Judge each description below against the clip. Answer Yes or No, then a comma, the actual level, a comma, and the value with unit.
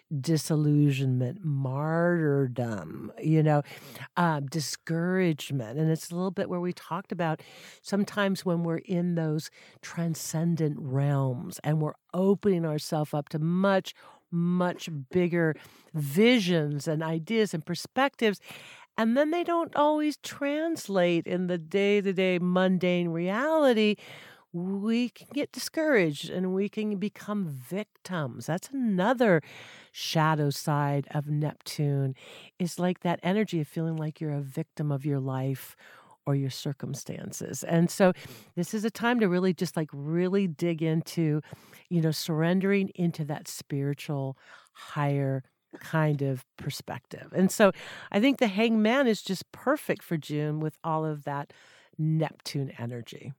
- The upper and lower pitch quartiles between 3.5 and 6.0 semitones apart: Yes, average, 4.3 semitones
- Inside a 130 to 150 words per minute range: Yes, slow, 135 wpm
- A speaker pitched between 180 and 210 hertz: No, medium, 165 Hz